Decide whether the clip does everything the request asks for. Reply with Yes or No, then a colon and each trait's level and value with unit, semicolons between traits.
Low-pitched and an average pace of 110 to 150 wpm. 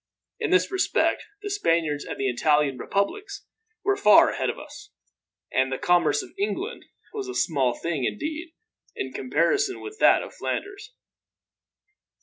No: very high, 300 Hz; average, 145 wpm